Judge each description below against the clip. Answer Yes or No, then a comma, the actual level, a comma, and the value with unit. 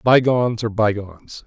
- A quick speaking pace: No, slow, 125 wpm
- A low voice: Yes, low, 110 Hz